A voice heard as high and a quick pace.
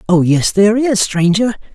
No: high, 200 Hz; average, 170 wpm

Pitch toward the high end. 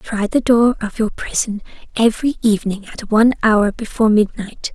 Yes: high, 220 Hz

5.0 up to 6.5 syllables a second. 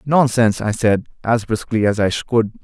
Yes: 5.1 syllables/s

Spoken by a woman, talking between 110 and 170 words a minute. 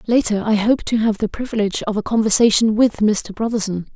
No: female; average, 195 wpm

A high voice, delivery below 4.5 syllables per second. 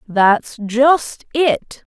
Yes: very high, 250 Hz; 1.9 syllables/s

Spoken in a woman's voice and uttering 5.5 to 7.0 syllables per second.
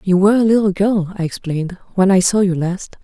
Yes: female; 6.0 syllables/s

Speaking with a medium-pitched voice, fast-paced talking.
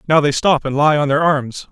Yes: medium, 145 Hz; fast, 280 wpm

